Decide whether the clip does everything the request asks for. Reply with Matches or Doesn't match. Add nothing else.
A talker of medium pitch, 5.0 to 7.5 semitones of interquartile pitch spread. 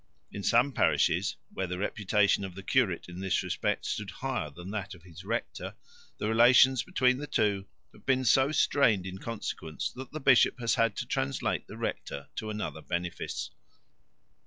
Doesn't match